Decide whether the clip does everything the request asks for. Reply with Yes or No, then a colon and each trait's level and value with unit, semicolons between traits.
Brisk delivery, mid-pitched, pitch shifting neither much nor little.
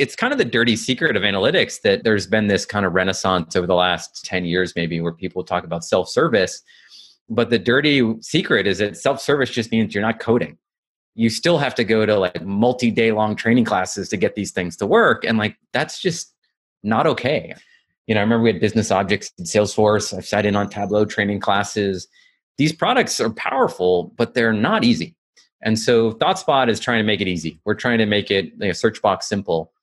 No: fast, 220 wpm; low, 105 Hz; average, 3.5 semitones